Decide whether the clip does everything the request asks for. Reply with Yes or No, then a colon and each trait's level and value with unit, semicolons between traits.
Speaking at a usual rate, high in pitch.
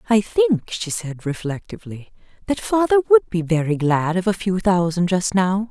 Yes: average, 180 wpm; high, 195 Hz